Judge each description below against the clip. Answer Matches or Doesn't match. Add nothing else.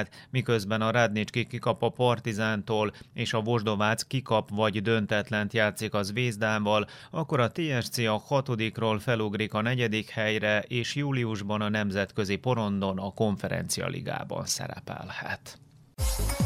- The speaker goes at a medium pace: Matches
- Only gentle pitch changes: Matches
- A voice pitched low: Matches